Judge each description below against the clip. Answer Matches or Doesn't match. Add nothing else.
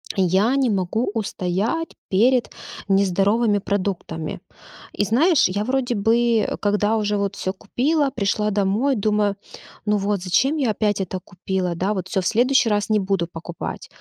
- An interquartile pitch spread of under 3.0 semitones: Doesn't match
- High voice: Matches